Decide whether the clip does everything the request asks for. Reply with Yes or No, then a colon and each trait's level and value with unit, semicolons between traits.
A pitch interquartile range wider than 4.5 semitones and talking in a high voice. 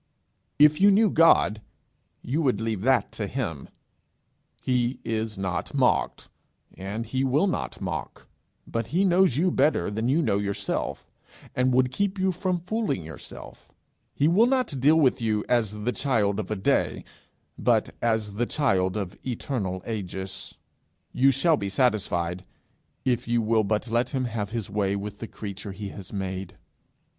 No: wide, 5.4 semitones; low, 115 Hz